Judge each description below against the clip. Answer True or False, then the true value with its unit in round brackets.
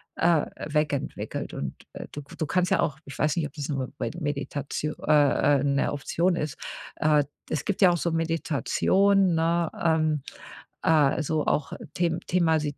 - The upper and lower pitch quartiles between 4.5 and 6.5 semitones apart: False (2.6 semitones)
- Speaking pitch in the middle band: True (155 Hz)